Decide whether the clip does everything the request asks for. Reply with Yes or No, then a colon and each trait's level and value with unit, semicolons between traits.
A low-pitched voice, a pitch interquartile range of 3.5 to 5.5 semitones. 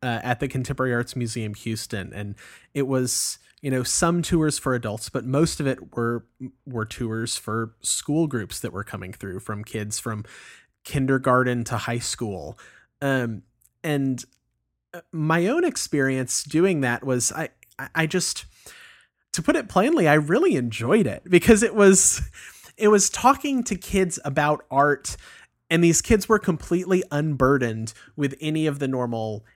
Yes: low, 130 Hz; average, 5.2 semitones